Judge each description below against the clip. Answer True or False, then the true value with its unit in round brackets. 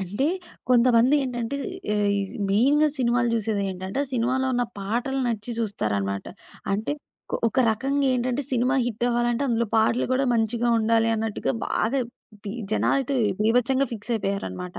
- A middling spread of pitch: True (3.3 semitones)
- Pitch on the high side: True (235 Hz)